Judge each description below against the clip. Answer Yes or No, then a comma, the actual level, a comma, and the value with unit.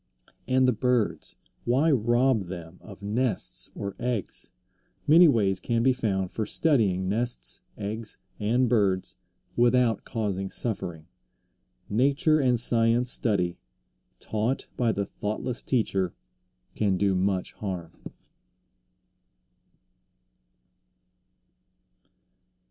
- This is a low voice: Yes, low, 110 Hz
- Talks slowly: Yes, slow, 100 wpm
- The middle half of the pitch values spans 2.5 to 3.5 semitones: No, average, 4.4 semitones